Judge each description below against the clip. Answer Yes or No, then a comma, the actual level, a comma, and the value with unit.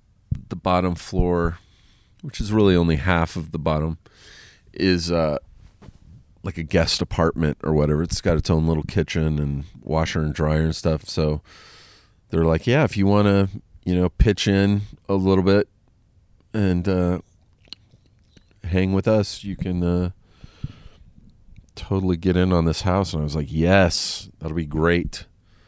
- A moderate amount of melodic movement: Yes, average, 3.2 semitones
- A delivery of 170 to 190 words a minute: No, average, 160 wpm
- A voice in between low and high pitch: No, very low, 90 Hz